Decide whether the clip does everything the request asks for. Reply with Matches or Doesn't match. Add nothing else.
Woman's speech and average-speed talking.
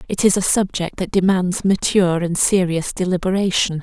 Matches